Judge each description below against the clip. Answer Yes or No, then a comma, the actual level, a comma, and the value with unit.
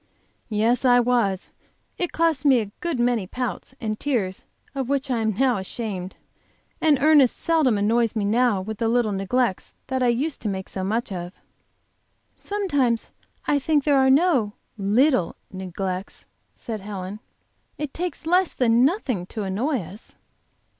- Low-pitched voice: No, high, 235 Hz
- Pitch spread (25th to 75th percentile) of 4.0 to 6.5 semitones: Yes, average, 5.1 semitones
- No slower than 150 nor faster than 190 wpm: Yes, average, 155 wpm